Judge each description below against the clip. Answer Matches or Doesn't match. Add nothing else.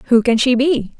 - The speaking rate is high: Matches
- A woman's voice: Matches